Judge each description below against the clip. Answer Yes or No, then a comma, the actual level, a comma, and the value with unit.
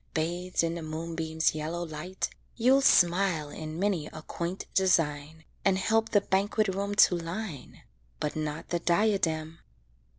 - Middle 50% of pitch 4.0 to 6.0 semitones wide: No, average, 3.5 semitones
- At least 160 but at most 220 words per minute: No, average, 140 wpm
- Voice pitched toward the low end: No, medium, 170 Hz